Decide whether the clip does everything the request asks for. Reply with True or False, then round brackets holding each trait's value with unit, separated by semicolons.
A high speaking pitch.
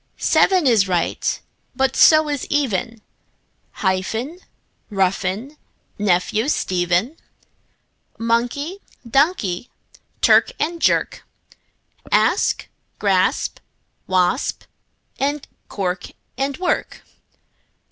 True (235 Hz)